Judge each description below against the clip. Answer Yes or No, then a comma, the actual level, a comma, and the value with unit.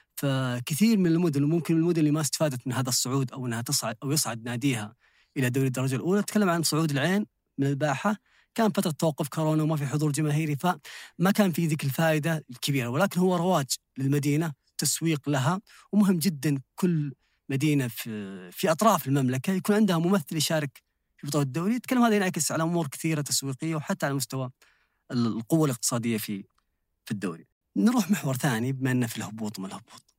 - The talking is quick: Yes, fast, 170 wpm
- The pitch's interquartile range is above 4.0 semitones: Yes, average, 4.5 semitones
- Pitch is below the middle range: No, medium, 150 Hz